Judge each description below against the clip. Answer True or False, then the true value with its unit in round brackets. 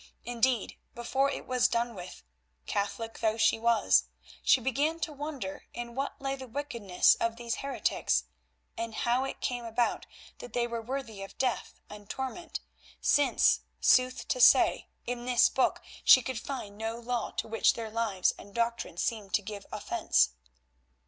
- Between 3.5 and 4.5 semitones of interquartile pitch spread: False (2.9 semitones)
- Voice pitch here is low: False (235 Hz)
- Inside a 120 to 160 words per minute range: True (155 wpm)